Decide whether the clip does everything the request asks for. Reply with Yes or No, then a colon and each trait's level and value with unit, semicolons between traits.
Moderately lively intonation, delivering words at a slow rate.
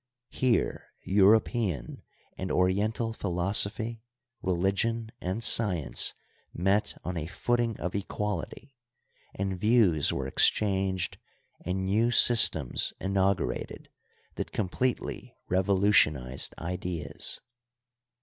Yes: average, 3.6 semitones; slow, 90 wpm